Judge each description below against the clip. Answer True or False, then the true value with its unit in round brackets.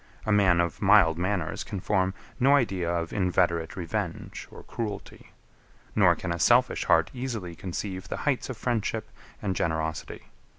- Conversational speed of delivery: True (155 wpm)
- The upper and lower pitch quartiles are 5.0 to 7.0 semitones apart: False (4.1 semitones)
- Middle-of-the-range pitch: False (95 Hz)